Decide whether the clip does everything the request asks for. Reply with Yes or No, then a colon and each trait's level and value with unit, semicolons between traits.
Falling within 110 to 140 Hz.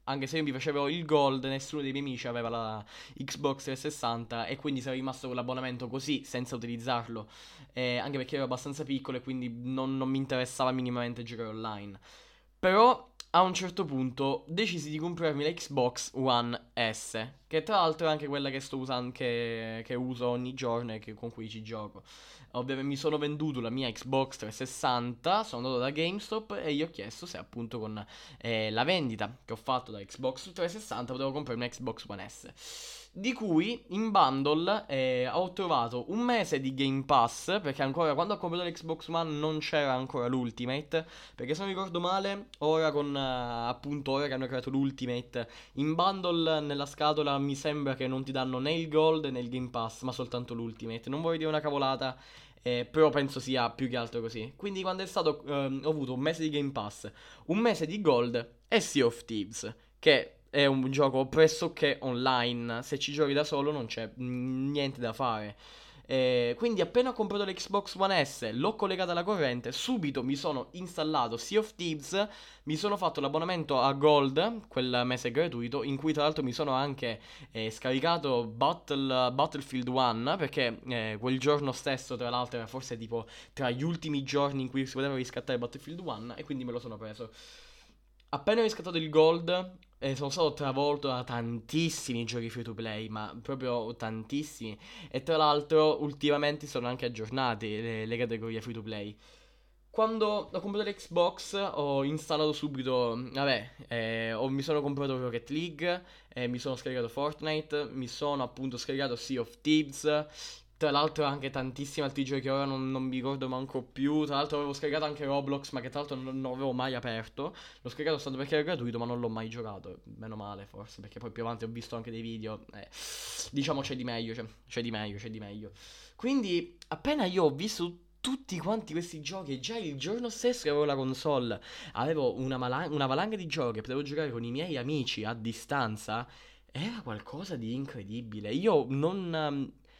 Yes: low, 135 Hz